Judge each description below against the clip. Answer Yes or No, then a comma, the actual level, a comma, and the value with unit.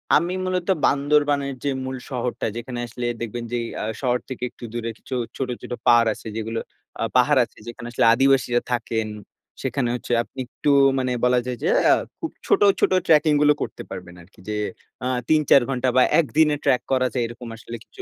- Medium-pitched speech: No, low, 125 Hz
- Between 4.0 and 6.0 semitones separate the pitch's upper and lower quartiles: No, average, 2.8 semitones